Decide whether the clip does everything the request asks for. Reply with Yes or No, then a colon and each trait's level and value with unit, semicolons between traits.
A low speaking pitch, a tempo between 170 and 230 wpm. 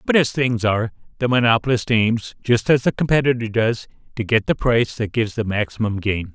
Yes: low, 115 Hz; average, 200 wpm